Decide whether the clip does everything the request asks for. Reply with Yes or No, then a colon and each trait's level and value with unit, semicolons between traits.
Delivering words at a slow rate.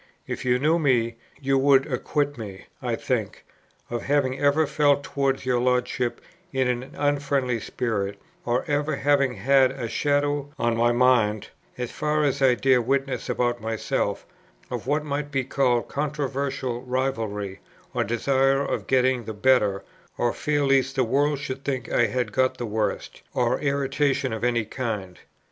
No: average, 160 wpm